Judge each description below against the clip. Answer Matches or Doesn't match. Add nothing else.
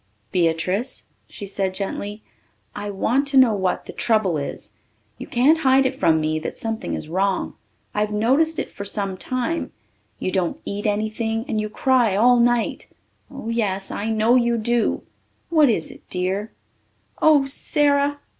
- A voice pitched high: Matches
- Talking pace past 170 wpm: Doesn't match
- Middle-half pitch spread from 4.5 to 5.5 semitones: Matches